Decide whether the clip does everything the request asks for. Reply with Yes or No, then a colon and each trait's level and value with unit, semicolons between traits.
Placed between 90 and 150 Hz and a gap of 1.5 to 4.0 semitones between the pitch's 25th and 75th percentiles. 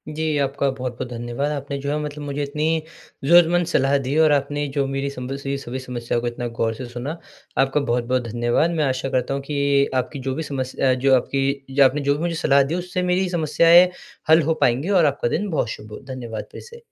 Yes: medium, 140 Hz; average, 2.9 semitones